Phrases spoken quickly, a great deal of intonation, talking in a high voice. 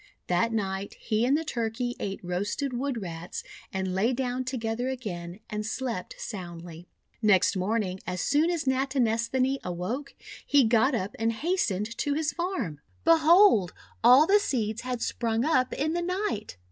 No: average, 155 wpm; wide, 5.7 semitones; high, 230 Hz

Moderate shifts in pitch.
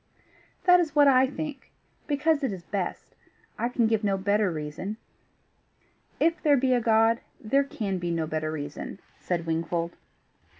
No: wide, 8.1 semitones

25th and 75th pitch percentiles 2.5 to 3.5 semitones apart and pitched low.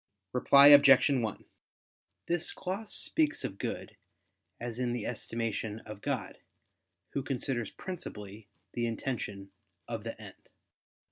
No: average, 4.5 semitones; low, 120 Hz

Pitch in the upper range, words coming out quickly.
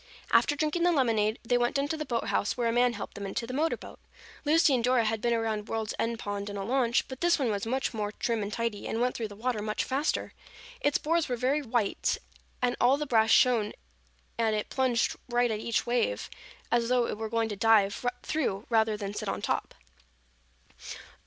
Yes: high, 235 Hz; fast, 220 wpm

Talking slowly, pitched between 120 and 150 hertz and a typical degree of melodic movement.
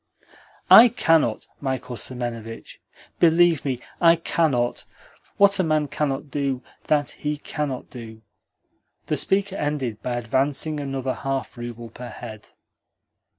Yes: slow, 120 wpm; low, 135 Hz; average, 4.1 semitones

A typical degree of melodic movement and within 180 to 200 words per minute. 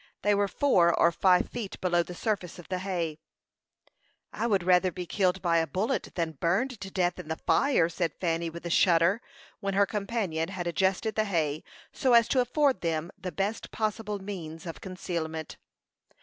Yes: average, 3.4 semitones; average, 185 wpm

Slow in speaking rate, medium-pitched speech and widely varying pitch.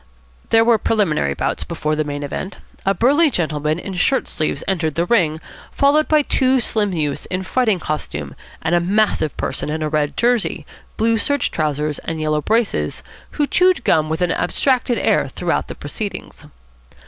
No: average, 170 wpm; medium, 180 Hz; wide, 7.2 semitones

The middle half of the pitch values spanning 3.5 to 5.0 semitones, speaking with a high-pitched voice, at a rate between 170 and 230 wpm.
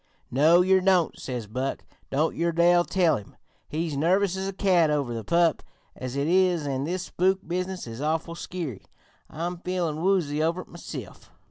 No: average, 3.9 semitones; medium, 170 Hz; average, 175 wpm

